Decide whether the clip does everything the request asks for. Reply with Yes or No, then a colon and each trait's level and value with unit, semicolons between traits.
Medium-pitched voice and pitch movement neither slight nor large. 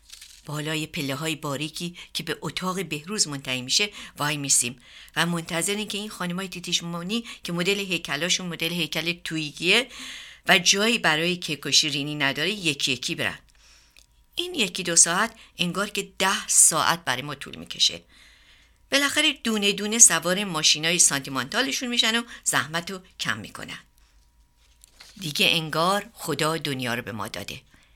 No: medium, 165 Hz; wide, 5.7 semitones